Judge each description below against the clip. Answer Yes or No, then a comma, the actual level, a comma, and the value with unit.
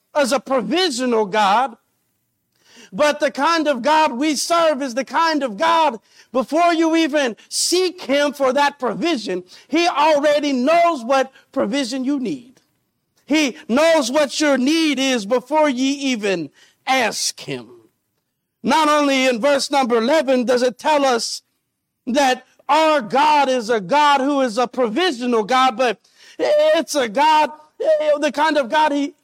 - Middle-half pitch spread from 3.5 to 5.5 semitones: No, average, 3.1 semitones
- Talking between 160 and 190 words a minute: No, average, 150 wpm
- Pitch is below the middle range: No, very high, 285 Hz